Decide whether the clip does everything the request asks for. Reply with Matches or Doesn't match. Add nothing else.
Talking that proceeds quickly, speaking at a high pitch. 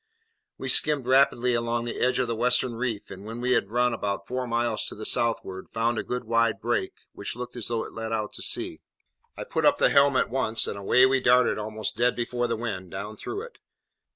Doesn't match